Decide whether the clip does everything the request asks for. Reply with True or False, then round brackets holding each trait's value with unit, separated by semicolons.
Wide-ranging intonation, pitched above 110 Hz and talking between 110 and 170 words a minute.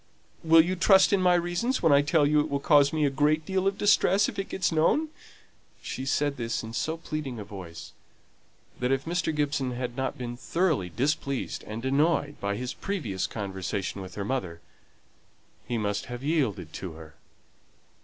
False (6.2 semitones; 140 Hz; 185 wpm)